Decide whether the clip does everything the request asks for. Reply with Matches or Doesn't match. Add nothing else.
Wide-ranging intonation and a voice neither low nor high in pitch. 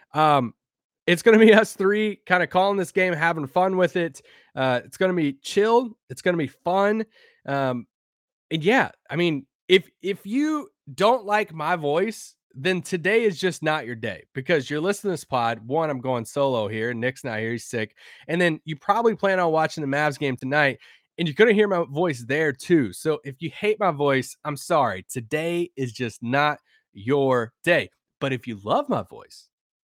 Matches